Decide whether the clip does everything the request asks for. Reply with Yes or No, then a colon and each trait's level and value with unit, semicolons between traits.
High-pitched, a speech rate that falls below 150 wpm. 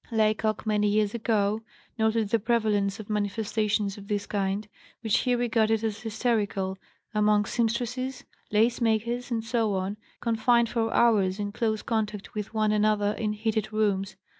Yes: high, 215 Hz; average, 140 wpm